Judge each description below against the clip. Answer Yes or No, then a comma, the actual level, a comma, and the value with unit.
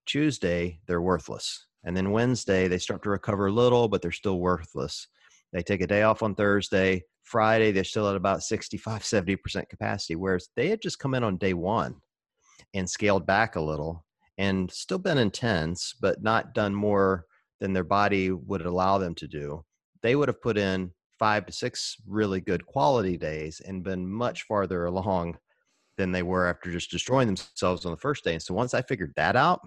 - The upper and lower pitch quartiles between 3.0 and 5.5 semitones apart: No, narrow, 2.6 semitones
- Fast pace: No, average, 195 wpm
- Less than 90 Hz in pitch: No, very low, 95 Hz